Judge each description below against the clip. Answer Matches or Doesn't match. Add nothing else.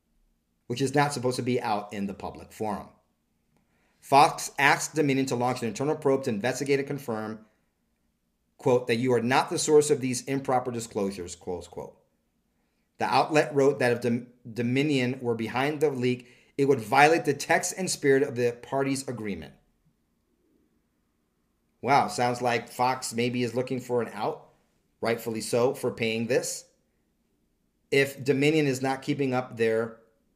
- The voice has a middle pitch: Doesn't match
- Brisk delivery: Doesn't match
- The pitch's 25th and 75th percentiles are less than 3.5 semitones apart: Matches